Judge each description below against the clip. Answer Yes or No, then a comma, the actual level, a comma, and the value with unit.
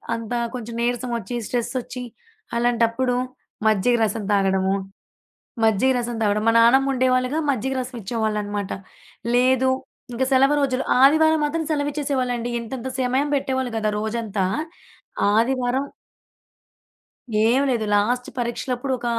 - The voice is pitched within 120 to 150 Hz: No, high, 245 Hz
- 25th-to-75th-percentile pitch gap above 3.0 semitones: No, average, 2.7 semitones